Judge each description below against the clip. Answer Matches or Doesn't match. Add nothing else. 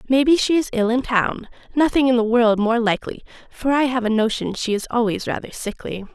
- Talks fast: Matches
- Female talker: Matches